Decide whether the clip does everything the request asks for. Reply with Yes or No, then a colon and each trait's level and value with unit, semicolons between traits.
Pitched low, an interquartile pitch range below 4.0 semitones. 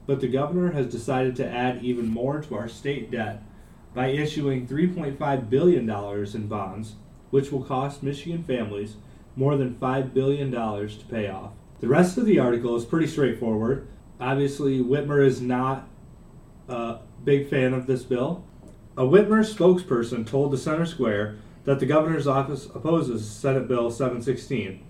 Yes: low, 130 Hz; average, 3.3 semitones